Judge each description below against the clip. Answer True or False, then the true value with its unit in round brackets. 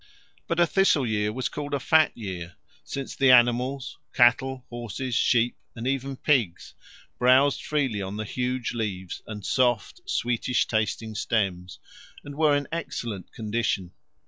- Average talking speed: True (145 wpm)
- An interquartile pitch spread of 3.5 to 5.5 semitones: True (3.9 semitones)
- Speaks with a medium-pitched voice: False (120 Hz)